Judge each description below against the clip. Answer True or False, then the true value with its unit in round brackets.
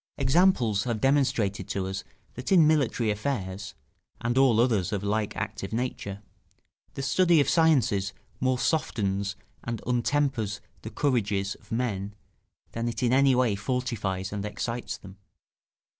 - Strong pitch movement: False (4.5 semitones)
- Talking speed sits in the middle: True (145 wpm)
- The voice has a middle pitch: False (115 Hz)